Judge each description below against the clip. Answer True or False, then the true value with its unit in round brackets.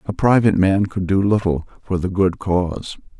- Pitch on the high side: False (95 Hz)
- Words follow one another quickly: False (190 wpm)